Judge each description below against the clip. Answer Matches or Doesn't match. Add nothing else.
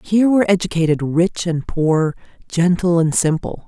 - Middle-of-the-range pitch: Matches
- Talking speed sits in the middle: Matches